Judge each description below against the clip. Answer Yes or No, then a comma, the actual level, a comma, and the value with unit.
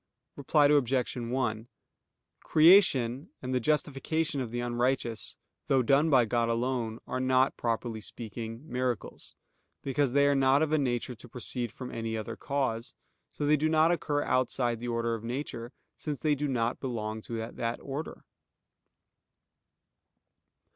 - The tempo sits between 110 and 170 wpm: Yes, average, 145 wpm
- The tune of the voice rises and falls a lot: No, average, 3.4 semitones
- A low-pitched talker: Yes, low, 125 Hz